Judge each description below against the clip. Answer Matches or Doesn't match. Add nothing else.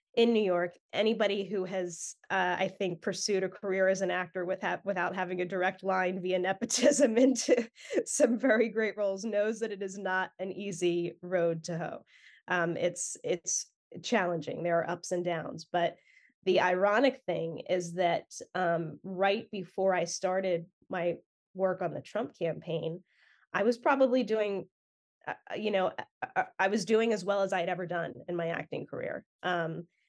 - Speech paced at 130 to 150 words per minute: Doesn't match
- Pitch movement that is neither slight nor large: Matches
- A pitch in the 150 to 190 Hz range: Matches